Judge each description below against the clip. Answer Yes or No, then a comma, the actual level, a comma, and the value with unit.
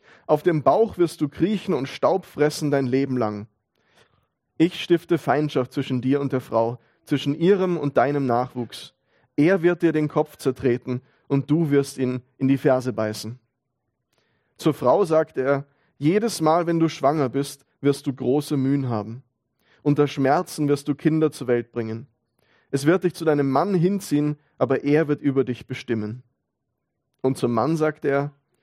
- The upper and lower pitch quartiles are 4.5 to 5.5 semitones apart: No, average, 3.5 semitones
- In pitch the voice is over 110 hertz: Yes, medium, 140 Hz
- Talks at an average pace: Yes, average, 170 wpm